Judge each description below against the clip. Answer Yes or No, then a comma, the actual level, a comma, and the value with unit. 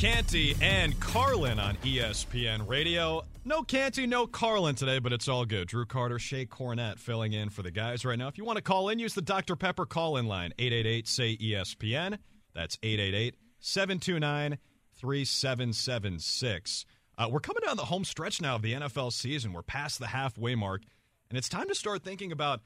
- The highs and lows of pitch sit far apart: Yes, wide, 6.3 semitones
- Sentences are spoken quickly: No, average, 170 wpm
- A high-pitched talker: No, low, 125 Hz